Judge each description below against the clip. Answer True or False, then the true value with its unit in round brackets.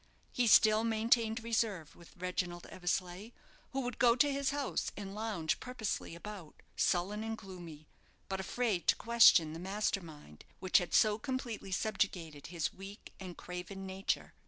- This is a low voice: False (195 Hz)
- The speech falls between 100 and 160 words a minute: True (155 wpm)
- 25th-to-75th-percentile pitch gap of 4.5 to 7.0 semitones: False (4.1 semitones)